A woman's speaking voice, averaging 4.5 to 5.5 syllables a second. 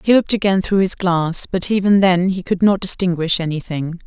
Yes: female; 5.4 syllables/s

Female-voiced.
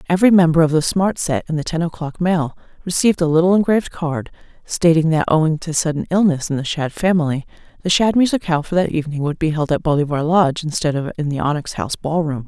Yes: female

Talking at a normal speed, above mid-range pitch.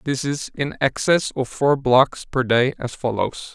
No: average, 185 wpm; low, 135 Hz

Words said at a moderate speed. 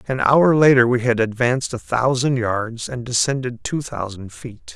Yes: average, 175 wpm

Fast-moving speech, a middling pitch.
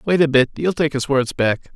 Yes: fast, 275 wpm; medium, 145 Hz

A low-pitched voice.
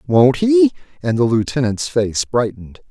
Yes: low, 125 Hz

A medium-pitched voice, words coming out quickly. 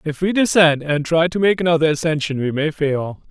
Yes: medium, 160 Hz; fast, 220 wpm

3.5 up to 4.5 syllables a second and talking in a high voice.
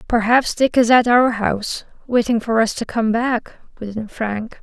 Yes: 4.4 syllables/s; high, 230 Hz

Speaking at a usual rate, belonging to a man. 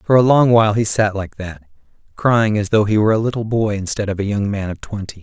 No: fast, 265 wpm; male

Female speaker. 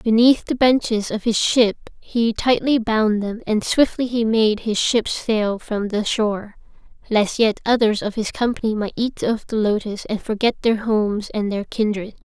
Yes: female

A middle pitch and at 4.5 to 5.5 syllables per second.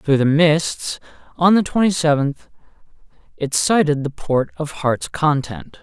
No: medium, 145 Hz; 4.0 syllables/s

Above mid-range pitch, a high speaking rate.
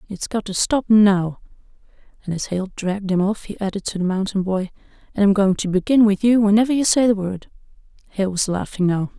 Yes: high, 200 Hz; fast, 215 wpm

